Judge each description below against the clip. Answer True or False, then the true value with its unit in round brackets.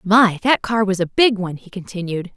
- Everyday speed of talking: False (230 wpm)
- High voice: True (200 Hz)